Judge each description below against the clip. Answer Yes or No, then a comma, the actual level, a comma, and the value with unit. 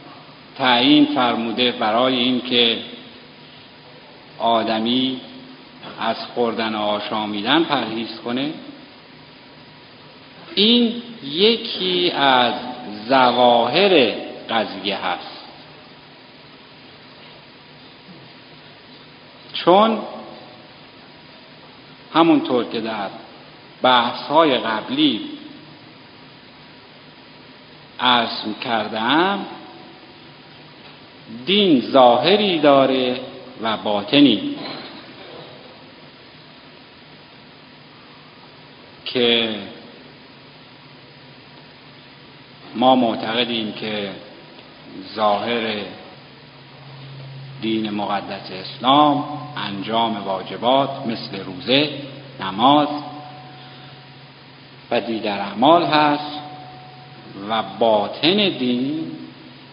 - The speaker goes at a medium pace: No, slow, 50 wpm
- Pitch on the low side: Yes, low, 130 Hz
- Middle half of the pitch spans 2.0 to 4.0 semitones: No, average, 4.6 semitones